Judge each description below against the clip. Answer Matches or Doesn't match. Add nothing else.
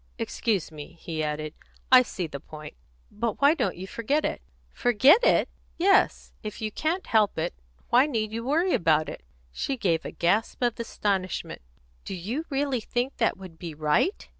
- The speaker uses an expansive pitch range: Matches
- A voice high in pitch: Matches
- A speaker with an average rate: Matches